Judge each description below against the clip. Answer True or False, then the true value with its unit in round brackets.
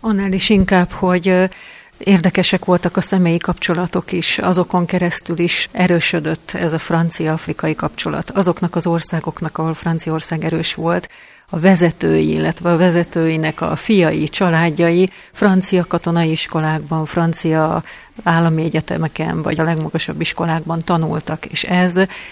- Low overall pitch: False (170 Hz)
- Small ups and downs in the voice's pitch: True (2.1 semitones)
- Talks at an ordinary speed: True (125 wpm)